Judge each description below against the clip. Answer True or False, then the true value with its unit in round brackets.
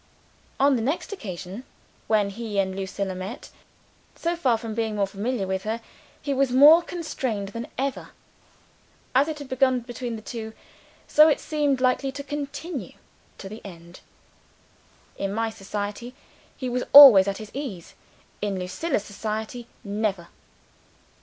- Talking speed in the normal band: True (145 wpm)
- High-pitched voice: True (230 Hz)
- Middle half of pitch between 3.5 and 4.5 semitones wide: False (5.3 semitones)